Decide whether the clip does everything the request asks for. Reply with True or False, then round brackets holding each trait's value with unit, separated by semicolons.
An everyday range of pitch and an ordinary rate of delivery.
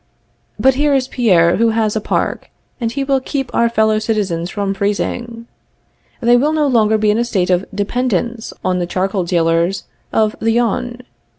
True (3.7 semitones; 185 wpm)